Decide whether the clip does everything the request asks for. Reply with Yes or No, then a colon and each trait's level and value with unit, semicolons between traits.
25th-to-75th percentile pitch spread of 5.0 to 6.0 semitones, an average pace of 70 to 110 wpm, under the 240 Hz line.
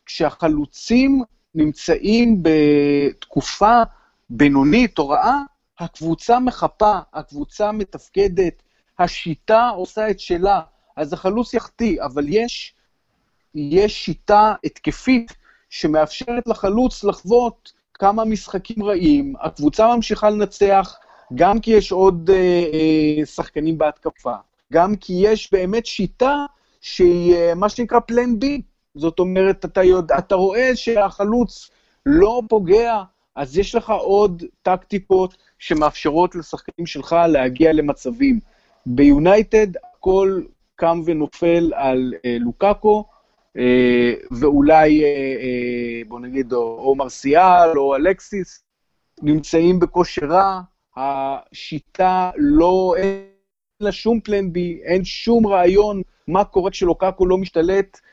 Yes: average, 5.3 semitones; average, 105 wpm; medium, 185 Hz